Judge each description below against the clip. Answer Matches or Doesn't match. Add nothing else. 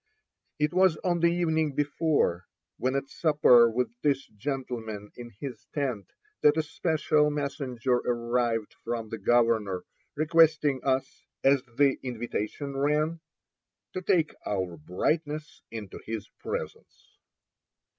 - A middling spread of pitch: Matches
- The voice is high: Doesn't match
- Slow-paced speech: Matches